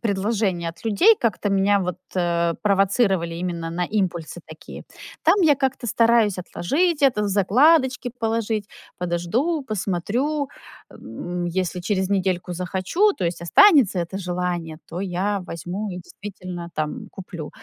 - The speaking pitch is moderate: No, high, 195 Hz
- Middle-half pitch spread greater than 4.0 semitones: Yes, average, 4.6 semitones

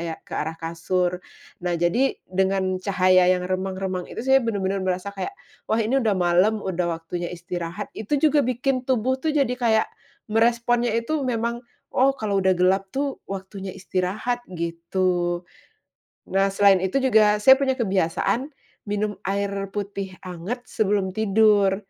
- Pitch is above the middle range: Yes, high, 195 Hz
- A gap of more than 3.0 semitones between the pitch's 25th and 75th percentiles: Yes, average, 4.1 semitones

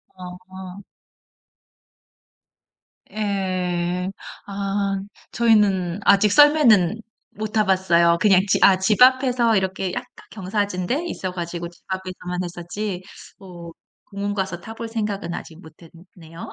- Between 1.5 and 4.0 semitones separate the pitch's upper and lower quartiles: Yes, average, 2.8 semitones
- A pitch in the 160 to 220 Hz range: Yes, high, 190 Hz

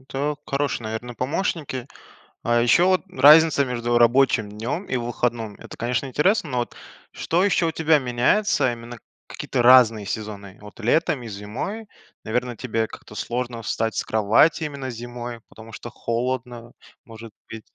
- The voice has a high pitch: No, low, 120 Hz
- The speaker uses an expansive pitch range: No, average, 3.5 semitones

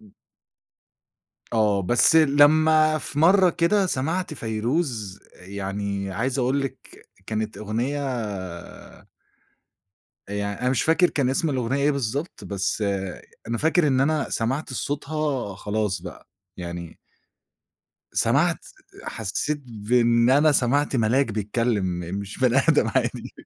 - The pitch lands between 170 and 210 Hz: No, low, 125 Hz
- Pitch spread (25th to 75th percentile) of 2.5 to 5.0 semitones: No, wide, 5.5 semitones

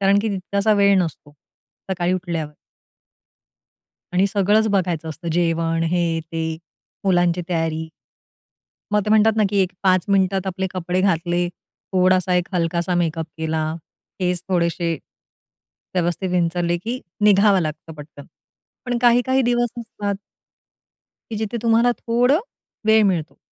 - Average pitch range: Yes, average, 3.4 semitones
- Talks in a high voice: No, medium, 180 Hz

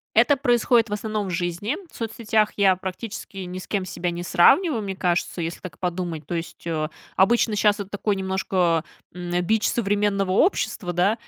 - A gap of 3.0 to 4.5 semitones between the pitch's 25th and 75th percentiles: Yes, average, 3.4 semitones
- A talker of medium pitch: No, high, 195 Hz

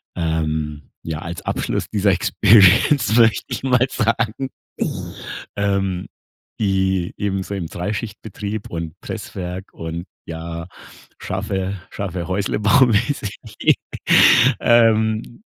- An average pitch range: Yes, average, 3.9 semitones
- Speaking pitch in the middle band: No, low, 100 Hz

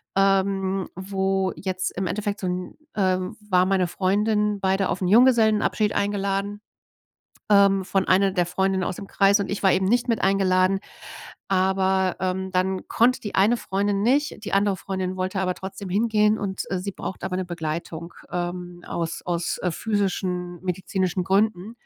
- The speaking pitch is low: No, high, 190 Hz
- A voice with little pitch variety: Yes, narrow, 1.6 semitones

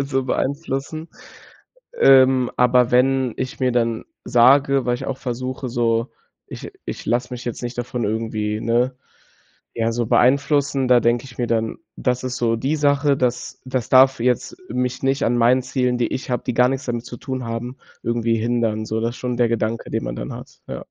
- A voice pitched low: Yes, low, 125 Hz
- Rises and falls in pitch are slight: Yes, narrow, 2.0 semitones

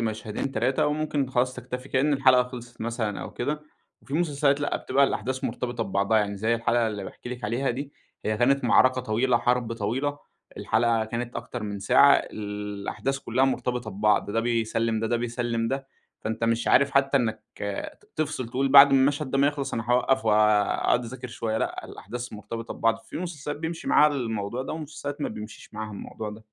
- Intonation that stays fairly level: No, average, 3.5 semitones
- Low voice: Yes, low, 120 Hz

